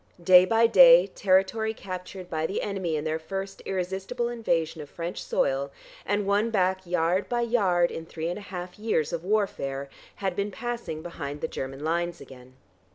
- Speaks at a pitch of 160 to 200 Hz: Yes, medium, 185 Hz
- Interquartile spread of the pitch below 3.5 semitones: No, average, 4.0 semitones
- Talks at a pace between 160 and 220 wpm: Yes, average, 175 wpm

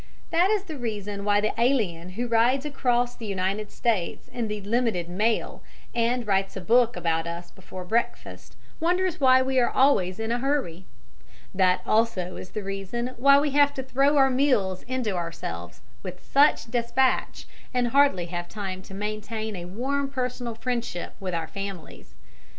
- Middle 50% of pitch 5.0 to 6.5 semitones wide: Yes, wide, 5.4 semitones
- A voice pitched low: No, high, 225 Hz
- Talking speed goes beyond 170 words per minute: No, average, 165 wpm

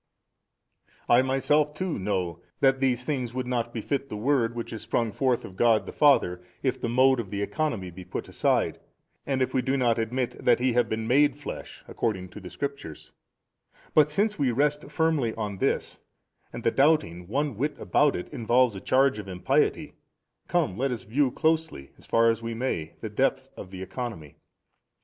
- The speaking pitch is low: Yes, low, 125 Hz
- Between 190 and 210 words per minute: Yes, average, 195 wpm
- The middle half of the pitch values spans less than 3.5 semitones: No, average, 4.3 semitones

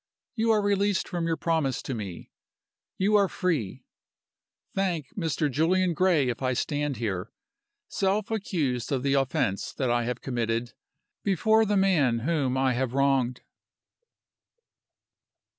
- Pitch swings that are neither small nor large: No, wide, 7.0 semitones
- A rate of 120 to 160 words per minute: Yes, slow, 135 wpm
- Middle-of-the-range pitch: Yes, medium, 145 Hz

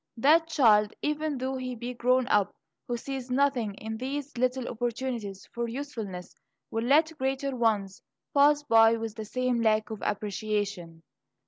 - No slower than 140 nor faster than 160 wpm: Yes, average, 150 wpm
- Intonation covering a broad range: No, average, 3.7 semitones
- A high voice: Yes, high, 240 Hz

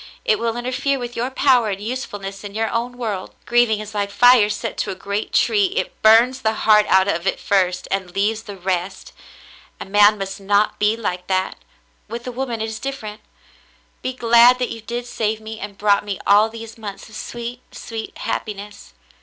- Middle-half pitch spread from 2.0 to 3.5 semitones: Yes, average, 2.9 semitones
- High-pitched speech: Yes, high, 220 Hz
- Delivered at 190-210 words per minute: Yes, average, 195 wpm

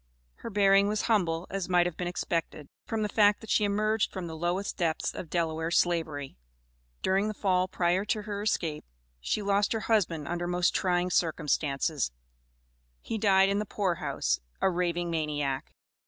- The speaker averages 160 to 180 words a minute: Yes, average, 170 wpm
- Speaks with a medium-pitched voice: Yes, medium, 180 Hz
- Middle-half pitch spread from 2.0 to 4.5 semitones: Yes, average, 3.6 semitones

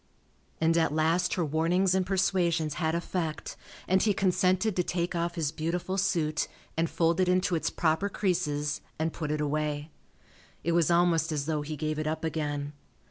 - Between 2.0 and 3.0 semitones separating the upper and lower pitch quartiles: Yes, average, 2.7 semitones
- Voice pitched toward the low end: No, medium, 165 Hz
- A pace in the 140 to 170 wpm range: No, average, 180 wpm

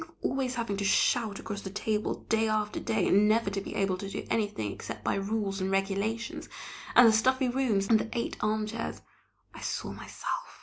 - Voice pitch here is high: Yes, high, 215 Hz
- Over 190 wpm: Yes, fast, 205 wpm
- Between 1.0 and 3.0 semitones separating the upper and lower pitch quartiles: Yes, narrow, 2.6 semitones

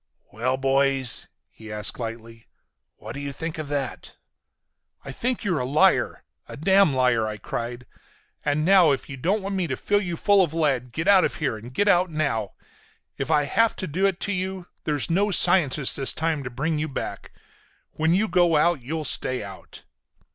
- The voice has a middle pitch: Yes, medium, 150 Hz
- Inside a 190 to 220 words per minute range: Yes, average, 195 wpm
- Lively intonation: Yes, wide, 5.7 semitones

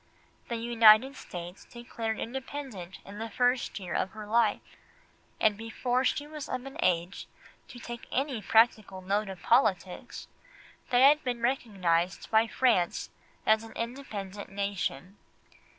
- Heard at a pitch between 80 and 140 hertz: No, high, 225 Hz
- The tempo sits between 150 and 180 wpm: No, average, 140 wpm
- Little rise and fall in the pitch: No, average, 4.0 semitones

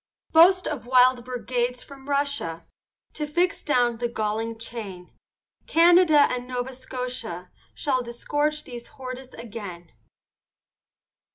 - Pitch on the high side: Yes, very high, 250 Hz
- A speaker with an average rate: No, slow, 110 wpm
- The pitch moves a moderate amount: Yes, average, 3.8 semitones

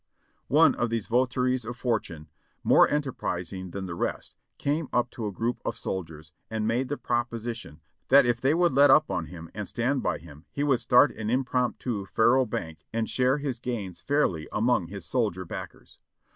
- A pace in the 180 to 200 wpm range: Yes, average, 185 wpm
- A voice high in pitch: No, low, 120 Hz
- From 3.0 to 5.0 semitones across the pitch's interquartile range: No, wide, 5.4 semitones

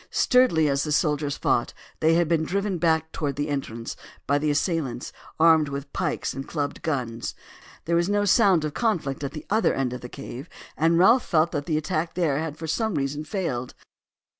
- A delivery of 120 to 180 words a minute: No, average, 195 wpm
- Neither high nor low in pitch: Yes, medium, 155 Hz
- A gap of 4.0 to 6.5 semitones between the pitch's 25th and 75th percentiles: No, average, 3.3 semitones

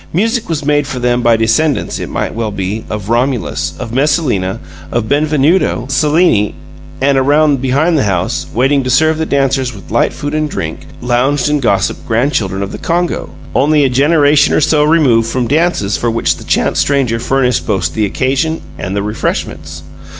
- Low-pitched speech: Yes, low, 130 Hz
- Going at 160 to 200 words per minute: Yes, average, 180 wpm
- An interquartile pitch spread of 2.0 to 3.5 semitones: No, average, 4.8 semitones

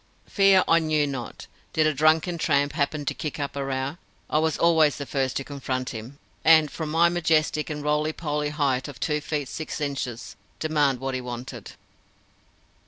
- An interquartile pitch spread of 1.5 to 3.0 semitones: Yes, narrow, 2.5 semitones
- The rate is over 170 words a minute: Yes, average, 180 wpm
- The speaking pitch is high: No, medium, 150 Hz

